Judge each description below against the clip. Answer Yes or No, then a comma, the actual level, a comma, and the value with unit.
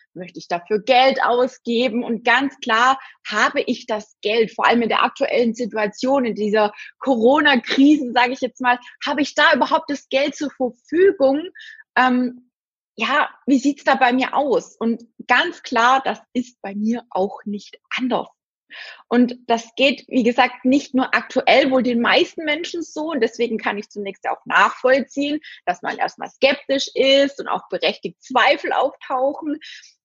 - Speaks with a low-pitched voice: No, very high, 255 Hz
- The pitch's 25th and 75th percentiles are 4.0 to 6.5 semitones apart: No, average, 3.1 semitones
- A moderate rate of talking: Yes, average, 165 wpm